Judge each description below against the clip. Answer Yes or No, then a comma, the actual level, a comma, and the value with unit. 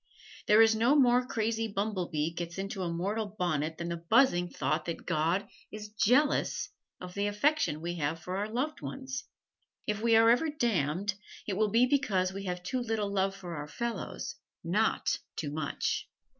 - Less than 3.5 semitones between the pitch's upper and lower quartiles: No, average, 4.7 semitones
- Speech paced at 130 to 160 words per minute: No, average, 175 wpm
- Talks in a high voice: Yes, high, 200 Hz